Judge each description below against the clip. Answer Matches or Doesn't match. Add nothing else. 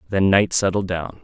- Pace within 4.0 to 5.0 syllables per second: Matches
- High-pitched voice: Doesn't match